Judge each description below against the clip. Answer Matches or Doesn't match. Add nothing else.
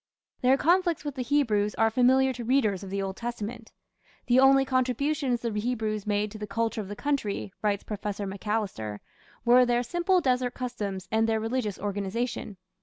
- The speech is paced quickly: Doesn't match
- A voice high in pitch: Matches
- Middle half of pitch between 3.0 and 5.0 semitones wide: Matches